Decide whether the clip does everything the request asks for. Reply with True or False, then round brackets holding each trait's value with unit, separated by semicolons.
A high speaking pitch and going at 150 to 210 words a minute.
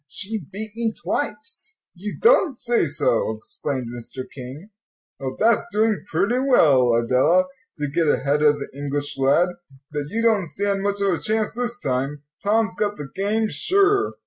True (195 Hz; 165 wpm)